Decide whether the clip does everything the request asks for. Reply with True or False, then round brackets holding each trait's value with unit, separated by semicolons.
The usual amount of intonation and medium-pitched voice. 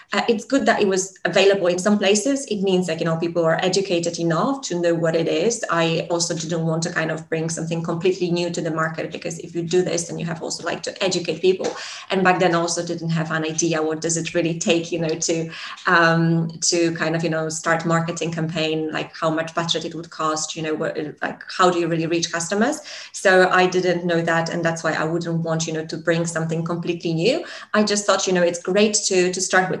False (2.0 semitones; 170 Hz)